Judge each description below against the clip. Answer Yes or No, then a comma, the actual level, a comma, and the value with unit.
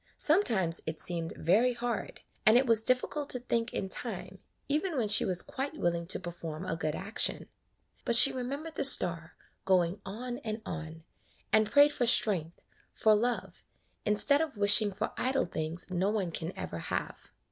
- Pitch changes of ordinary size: No, wide, 6.3 semitones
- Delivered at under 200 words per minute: Yes, average, 170 wpm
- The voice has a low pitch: No, high, 215 Hz